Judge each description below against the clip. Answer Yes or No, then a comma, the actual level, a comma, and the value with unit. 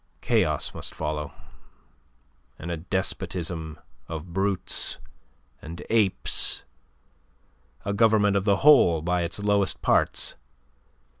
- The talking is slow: Yes, slow, 100 wpm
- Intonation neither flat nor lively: Yes, average, 3.4 semitones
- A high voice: No, very low, 95 Hz